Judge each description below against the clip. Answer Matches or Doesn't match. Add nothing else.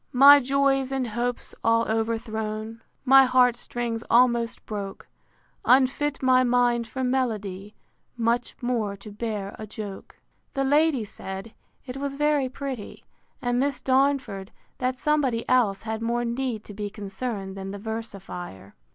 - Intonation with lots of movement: Doesn't match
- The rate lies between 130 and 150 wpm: Matches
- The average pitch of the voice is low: Doesn't match